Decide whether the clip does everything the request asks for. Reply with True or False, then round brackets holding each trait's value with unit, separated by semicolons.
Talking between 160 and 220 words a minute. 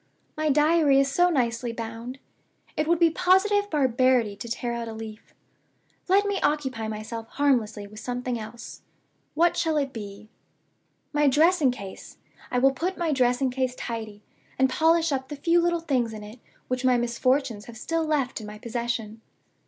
True (170 wpm)